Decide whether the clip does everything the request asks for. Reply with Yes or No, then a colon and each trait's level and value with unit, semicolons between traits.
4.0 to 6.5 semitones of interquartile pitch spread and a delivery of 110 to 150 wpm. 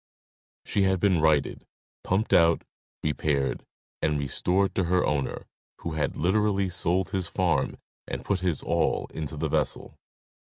No: average, 3.5 semitones; average, 140 wpm